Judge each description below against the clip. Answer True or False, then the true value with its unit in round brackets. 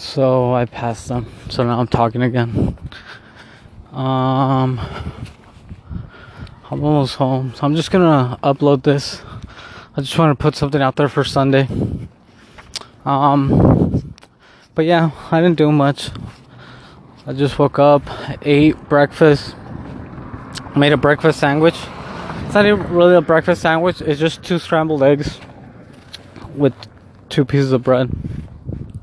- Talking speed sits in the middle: False (130 wpm)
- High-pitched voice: False (140 Hz)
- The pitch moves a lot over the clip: False (3.1 semitones)